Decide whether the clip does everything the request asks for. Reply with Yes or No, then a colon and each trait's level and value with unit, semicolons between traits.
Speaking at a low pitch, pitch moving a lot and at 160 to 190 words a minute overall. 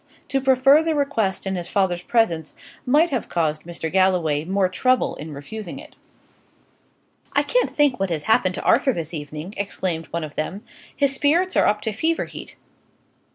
No: high, 195 Hz; wide, 8.1 semitones; average, 175 wpm